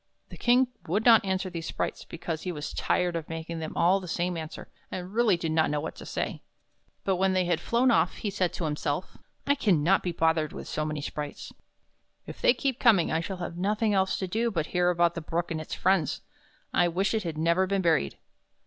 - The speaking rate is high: Yes, fast, 230 wpm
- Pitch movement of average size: Yes, average, 3.1 semitones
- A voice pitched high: No, medium, 175 Hz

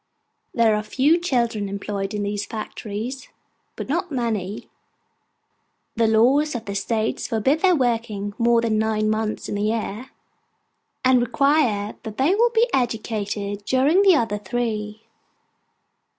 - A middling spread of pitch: Yes, average, 3.7 semitones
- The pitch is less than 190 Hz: No, high, 225 Hz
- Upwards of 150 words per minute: No, slow, 135 wpm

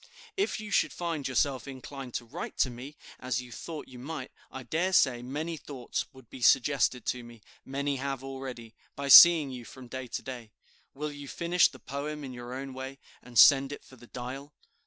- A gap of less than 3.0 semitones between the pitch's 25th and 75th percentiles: Yes, narrow, 2.5 semitones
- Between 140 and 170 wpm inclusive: No, average, 200 wpm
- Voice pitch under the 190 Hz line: Yes, low, 135 Hz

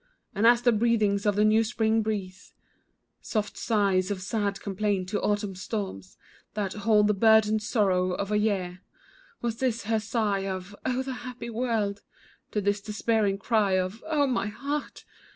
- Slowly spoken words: No, average, 165 wpm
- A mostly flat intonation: Yes, narrow, 2.2 semitones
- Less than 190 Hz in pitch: No, high, 210 Hz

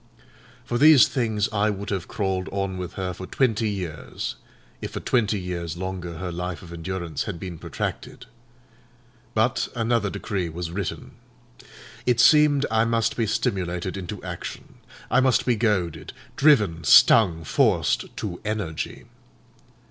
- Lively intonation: No, average, 4.1 semitones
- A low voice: Yes, very low, 95 Hz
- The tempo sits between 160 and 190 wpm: No, average, 140 wpm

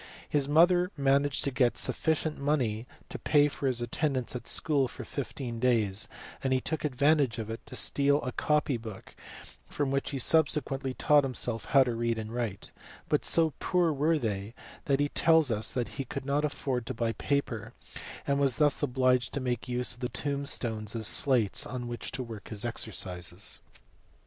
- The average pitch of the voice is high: No, low, 130 Hz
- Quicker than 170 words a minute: Yes, average, 180 wpm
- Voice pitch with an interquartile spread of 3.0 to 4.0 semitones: Yes, average, 3.6 semitones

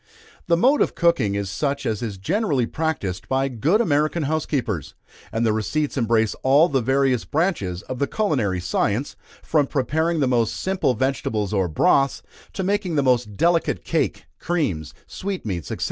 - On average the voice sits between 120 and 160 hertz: Yes, low, 135 Hz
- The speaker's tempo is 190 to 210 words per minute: No, average, 160 wpm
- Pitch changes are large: Yes, wide, 6.7 semitones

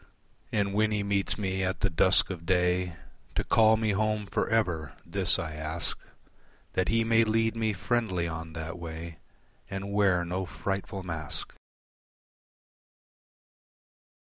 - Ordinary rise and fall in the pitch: Yes, average, 4.0 semitones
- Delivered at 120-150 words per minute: Yes, average, 140 wpm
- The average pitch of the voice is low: Yes, very low, 95 Hz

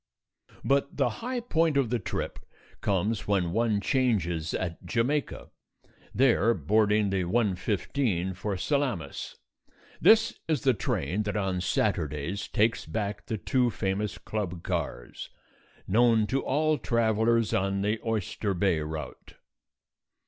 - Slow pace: Yes, slow, 125 wpm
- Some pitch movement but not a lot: Yes, average, 4.4 semitones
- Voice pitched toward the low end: Yes, low, 105 Hz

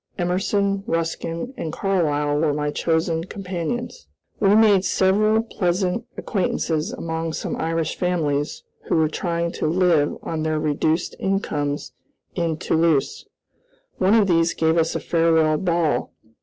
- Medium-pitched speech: Yes, medium, 165 Hz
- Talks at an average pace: No, slow, 130 wpm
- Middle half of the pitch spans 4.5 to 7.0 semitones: No, average, 3.2 semitones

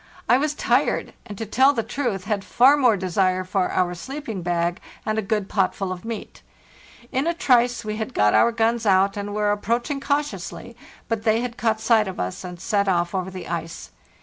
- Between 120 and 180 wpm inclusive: No, average, 200 wpm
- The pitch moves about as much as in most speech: Yes, average, 4.1 semitones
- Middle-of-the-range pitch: No, high, 210 Hz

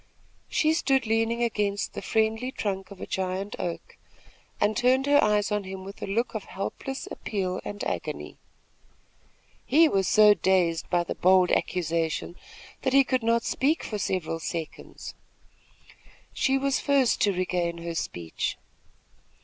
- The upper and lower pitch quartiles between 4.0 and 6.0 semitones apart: Yes, average, 4.9 semitones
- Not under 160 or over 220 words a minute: No, average, 150 wpm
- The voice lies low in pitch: No, high, 205 Hz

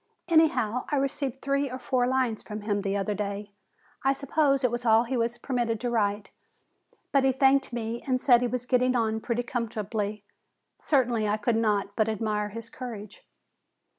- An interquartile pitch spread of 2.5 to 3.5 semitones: Yes, average, 3.2 semitones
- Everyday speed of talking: Yes, average, 180 wpm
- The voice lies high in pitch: Yes, high, 235 Hz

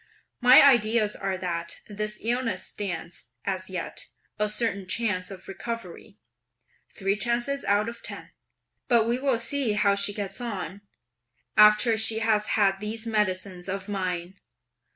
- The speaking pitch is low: No, high, 210 Hz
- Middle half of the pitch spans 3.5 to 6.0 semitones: No, average, 3.1 semitones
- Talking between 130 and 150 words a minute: Yes, average, 140 wpm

